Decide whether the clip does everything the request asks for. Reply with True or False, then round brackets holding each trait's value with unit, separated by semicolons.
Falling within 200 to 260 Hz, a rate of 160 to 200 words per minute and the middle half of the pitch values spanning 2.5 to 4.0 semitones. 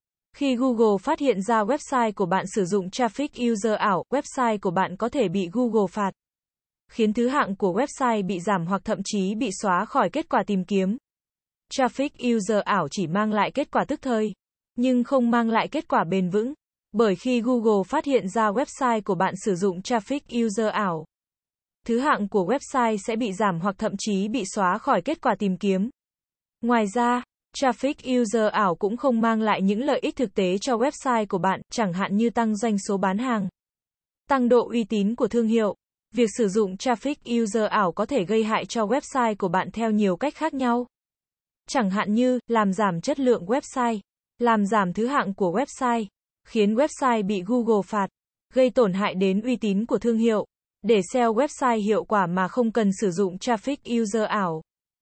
True (225 Hz; 195 wpm; 3.6 semitones)